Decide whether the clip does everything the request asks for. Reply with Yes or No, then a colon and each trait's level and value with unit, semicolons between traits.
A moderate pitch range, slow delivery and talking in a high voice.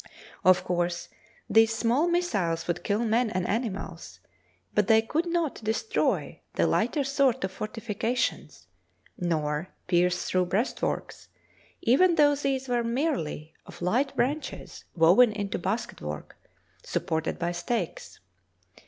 No: wide, 6.9 semitones; slow, 125 wpm; high, 220 Hz